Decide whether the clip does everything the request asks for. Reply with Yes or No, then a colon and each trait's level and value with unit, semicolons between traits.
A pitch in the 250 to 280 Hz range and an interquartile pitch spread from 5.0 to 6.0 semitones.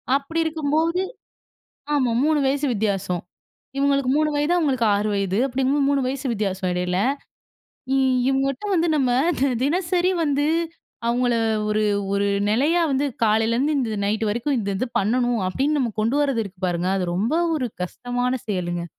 Yes: very high, 255 Hz; average, 5.3 semitones